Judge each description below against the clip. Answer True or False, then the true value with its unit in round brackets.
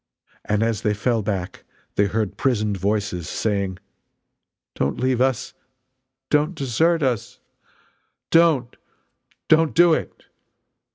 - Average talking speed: False (110 wpm)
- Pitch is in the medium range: False (115 Hz)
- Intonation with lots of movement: True (6.0 semitones)